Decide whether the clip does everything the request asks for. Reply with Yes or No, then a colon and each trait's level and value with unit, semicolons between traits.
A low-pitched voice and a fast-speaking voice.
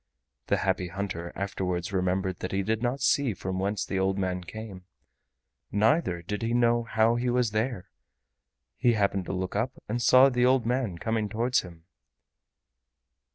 No: low, 105 Hz; average, 160 wpm